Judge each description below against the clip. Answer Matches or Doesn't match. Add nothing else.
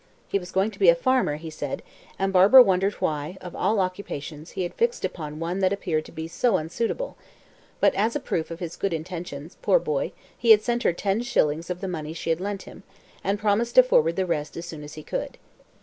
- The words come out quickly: Matches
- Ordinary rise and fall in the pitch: Matches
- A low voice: Doesn't match